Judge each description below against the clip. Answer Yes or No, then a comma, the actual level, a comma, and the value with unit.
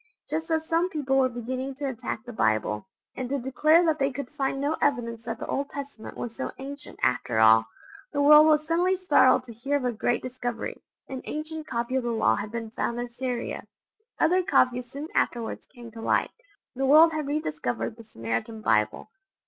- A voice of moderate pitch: No, very high, 255 Hz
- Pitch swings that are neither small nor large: Yes, average, 4.2 semitones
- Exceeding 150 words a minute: Yes, average, 195 wpm